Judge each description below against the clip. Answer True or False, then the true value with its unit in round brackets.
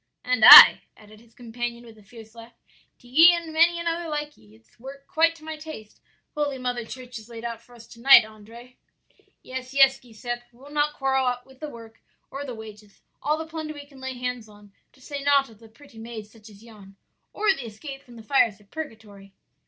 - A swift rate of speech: True (215 wpm)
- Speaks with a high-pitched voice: True (245 Hz)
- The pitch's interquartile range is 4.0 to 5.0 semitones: True (4.3 semitones)